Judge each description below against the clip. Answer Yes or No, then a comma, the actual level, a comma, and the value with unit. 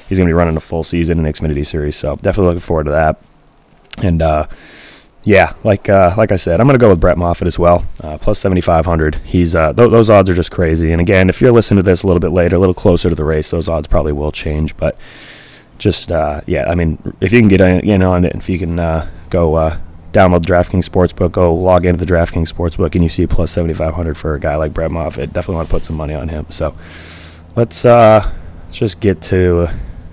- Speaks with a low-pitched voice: Yes, very low, 85 Hz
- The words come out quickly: Yes, fast, 245 wpm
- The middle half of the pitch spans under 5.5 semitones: Yes, narrow, 2.5 semitones